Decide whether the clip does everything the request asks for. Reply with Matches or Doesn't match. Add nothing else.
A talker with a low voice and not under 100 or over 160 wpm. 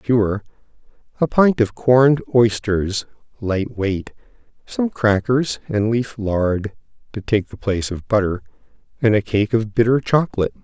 Matches